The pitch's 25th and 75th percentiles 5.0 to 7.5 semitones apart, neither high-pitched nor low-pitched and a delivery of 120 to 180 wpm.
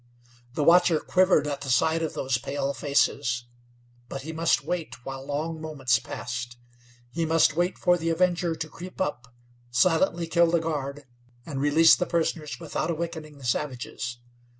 No: average, 3.7 semitones; medium, 155 Hz; average, 160 wpm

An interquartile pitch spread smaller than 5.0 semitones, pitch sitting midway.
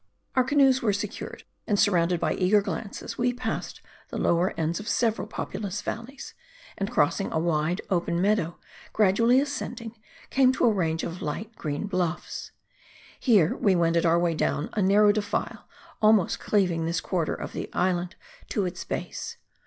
No: average, 4.3 semitones; high, 195 Hz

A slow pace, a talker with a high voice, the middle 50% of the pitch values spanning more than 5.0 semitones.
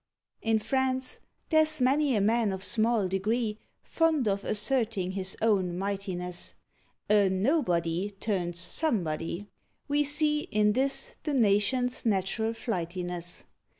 Yes: slow, 115 wpm; high, 210 Hz; wide, 5.4 semitones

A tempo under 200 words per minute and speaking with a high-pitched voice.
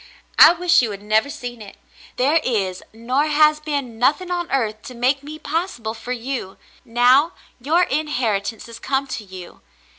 Yes: average, 175 wpm; very high, 255 Hz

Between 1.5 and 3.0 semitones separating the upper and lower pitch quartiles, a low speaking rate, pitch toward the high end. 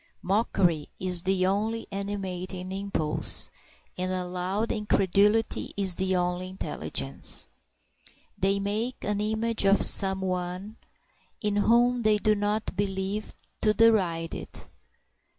Yes: narrow, 2.4 semitones; slow, 115 wpm; high, 195 Hz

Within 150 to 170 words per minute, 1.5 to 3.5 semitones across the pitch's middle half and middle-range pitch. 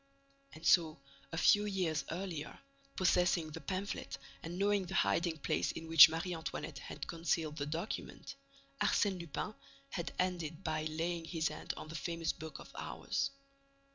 Yes: average, 155 wpm; narrow, 2.4 semitones; medium, 165 Hz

